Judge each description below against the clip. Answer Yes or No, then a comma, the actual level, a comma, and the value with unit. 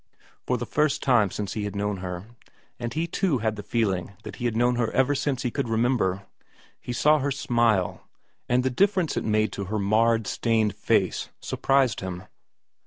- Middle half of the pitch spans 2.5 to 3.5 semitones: No, average, 4.2 semitones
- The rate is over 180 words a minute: Yes, average, 190 wpm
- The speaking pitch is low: Yes, low, 115 Hz